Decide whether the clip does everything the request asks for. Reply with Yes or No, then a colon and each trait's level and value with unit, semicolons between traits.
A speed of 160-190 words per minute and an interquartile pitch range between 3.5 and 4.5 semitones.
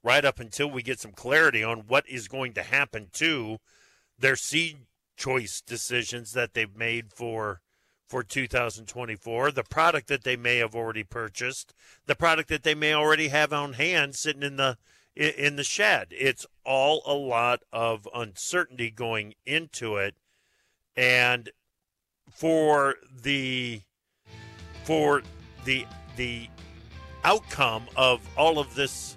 No: average, 140 wpm; average, 4.1 semitones